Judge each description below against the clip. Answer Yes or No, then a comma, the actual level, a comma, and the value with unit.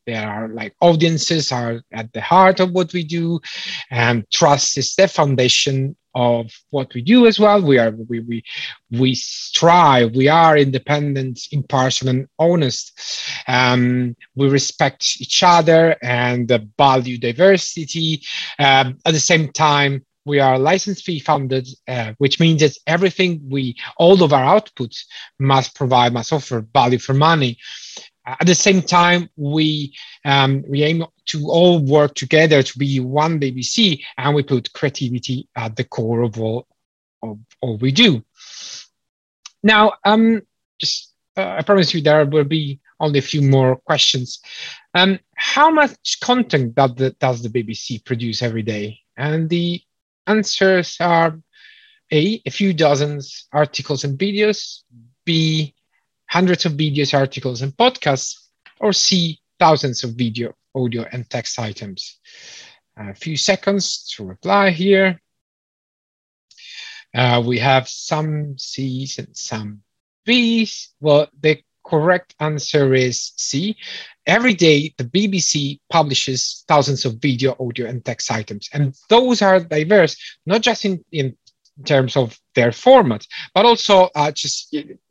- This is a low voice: No, medium, 145 Hz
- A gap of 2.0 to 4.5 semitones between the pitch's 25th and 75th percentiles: No, average, 5.2 semitones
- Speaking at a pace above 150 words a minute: No, average, 140 wpm